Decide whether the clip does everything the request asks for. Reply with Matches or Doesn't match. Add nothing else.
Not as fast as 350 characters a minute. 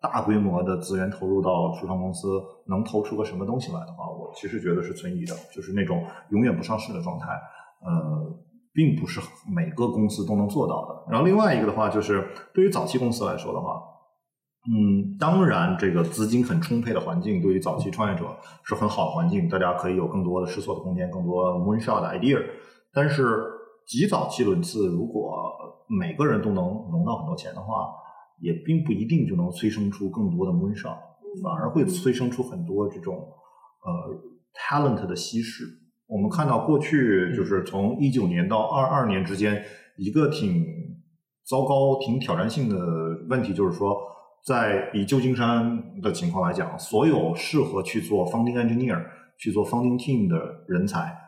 Matches